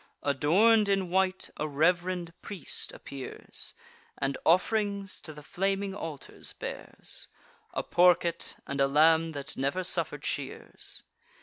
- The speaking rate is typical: No, slow, 120 wpm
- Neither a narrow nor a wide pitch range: Yes, average, 4.4 semitones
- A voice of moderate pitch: Yes, medium, 175 Hz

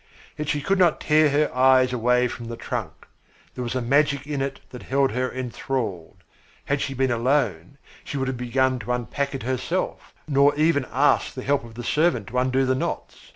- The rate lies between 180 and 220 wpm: Yes, fast, 205 wpm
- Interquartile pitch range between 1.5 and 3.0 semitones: Yes, narrow, 2.4 semitones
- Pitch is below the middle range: Yes, low, 130 Hz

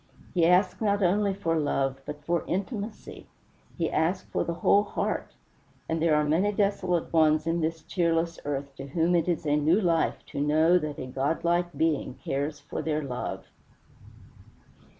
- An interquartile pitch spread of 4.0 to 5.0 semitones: No, average, 3.0 semitones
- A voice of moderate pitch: Yes, medium, 165 Hz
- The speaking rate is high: No, average, 170 wpm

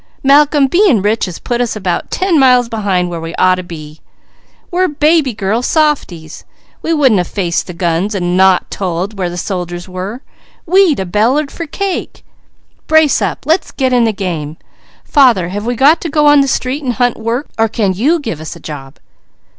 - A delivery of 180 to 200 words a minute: Yes, average, 195 wpm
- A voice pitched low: No, high, 225 Hz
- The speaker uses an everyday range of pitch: No, wide, 8.1 semitones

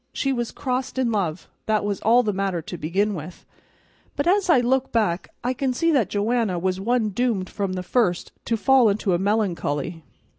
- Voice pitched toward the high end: Yes, high, 215 Hz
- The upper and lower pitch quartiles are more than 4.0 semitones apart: Yes, average, 5.0 semitones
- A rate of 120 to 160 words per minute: No, average, 195 wpm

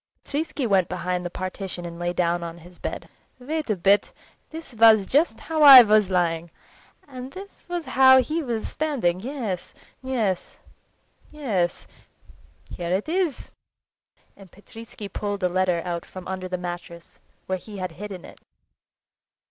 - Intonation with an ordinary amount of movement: No, wide, 6.6 semitones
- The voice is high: Yes, high, 195 Hz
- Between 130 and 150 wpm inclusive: Yes, average, 140 wpm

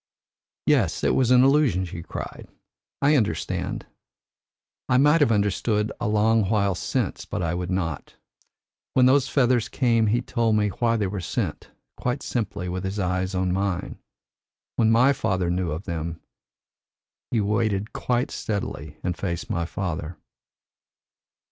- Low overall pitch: Yes, low, 105 Hz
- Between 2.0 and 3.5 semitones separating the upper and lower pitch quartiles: No, average, 4.8 semitones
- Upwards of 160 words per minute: No, average, 150 wpm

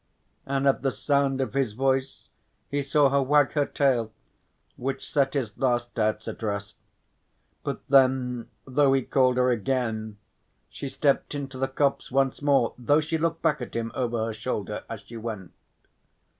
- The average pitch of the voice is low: Yes, low, 130 Hz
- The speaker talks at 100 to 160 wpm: No, average, 170 wpm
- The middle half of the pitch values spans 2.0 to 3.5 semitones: Yes, average, 3.0 semitones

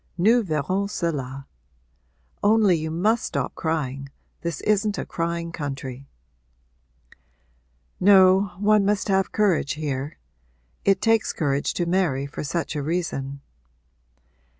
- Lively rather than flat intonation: Yes, wide, 5.8 semitones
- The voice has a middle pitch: Yes, medium, 170 Hz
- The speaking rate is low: Yes, slow, 115 wpm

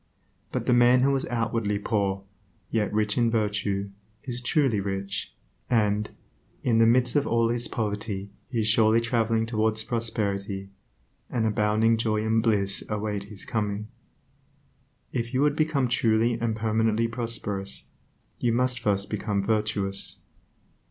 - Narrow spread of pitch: Yes, narrow, 2.2 semitones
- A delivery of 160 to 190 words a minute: No, average, 140 wpm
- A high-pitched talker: No, low, 110 Hz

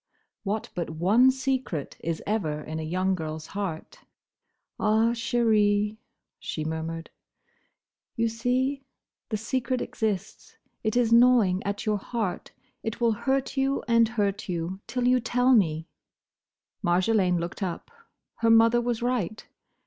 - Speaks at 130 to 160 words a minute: Yes, slow, 135 wpm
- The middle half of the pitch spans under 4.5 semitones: No, average, 5.0 semitones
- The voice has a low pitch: No, high, 215 Hz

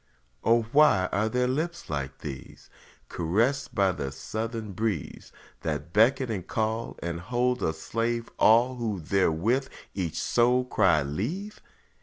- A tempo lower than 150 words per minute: Yes, slow, 135 wpm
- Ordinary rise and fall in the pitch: No, wide, 5.7 semitones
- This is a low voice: Yes, low, 110 Hz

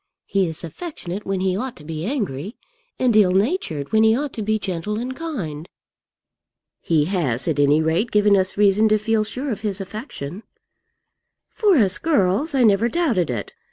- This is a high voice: Yes, high, 205 Hz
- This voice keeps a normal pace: Yes, average, 180 wpm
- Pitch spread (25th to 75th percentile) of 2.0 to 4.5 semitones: No, average, 5.1 semitones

